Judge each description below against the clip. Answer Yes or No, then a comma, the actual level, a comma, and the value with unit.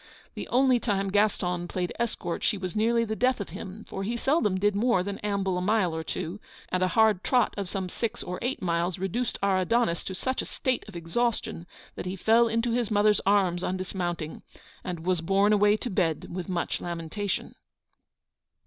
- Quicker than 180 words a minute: Yes, average, 195 wpm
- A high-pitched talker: Yes, high, 195 Hz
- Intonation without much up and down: No, average, 3.8 semitones